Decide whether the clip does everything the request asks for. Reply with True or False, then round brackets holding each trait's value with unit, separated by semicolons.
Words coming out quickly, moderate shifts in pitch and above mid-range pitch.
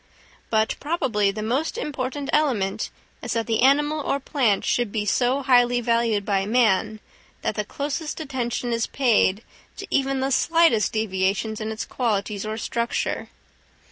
False (150 wpm; 4.1 semitones; 235 Hz)